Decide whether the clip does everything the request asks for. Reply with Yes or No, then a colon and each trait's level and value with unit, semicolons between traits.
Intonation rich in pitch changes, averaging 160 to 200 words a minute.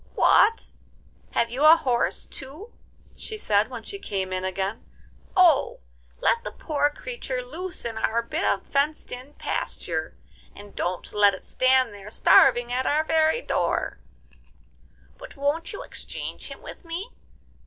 No: wide, 6.8 semitones; average, 150 wpm